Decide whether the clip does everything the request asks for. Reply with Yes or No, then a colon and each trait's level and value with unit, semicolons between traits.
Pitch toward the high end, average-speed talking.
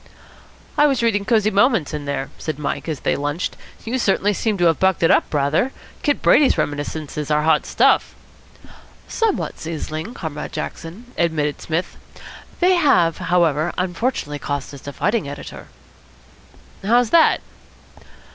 No: medium, 170 Hz; average, 145 wpm